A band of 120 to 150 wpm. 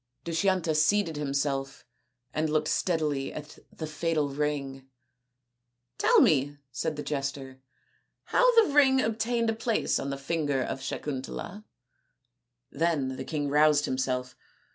Yes: slow, 135 wpm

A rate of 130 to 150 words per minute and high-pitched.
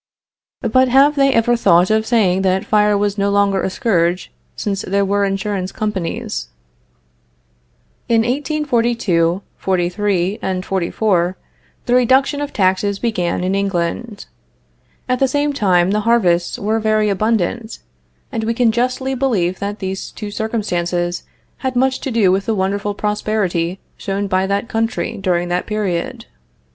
Yes: average, 145 wpm; high, 205 Hz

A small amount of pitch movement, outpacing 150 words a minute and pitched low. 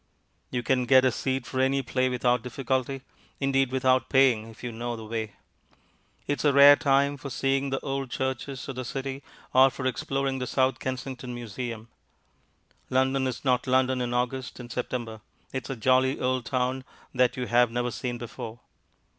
Yes: narrow, 1.6 semitones; average, 180 wpm; low, 130 Hz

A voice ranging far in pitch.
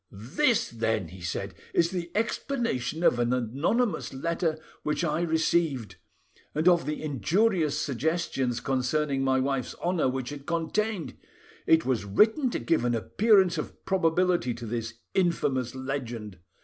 Yes: wide, 5.8 semitones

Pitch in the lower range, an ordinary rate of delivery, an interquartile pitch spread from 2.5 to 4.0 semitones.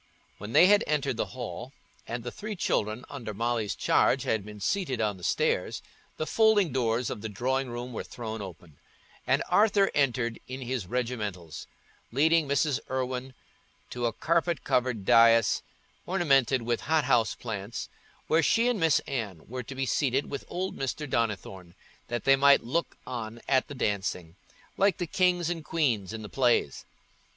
No: low, 125 Hz; average, 170 wpm; average, 4.7 semitones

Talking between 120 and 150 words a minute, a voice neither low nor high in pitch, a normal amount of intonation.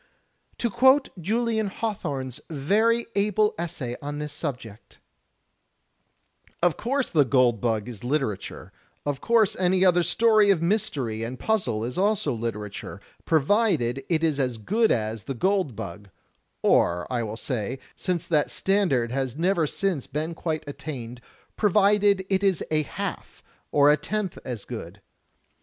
No: average, 145 wpm; medium, 155 Hz; wide, 8.4 semitones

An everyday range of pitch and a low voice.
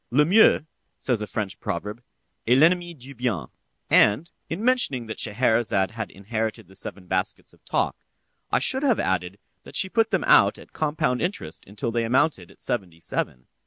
No: wide, 7.8 semitones; low, 115 Hz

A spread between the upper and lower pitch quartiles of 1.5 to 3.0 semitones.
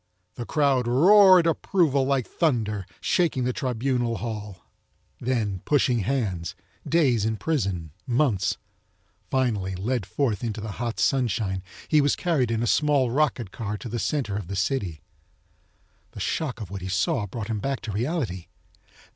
No: average, 5.2 semitones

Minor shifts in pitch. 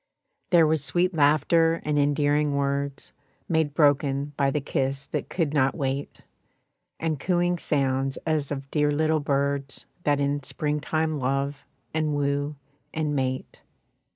Yes: narrow, 2.0 semitones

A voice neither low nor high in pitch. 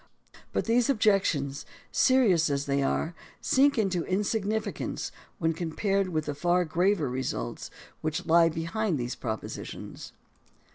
Yes: medium, 175 Hz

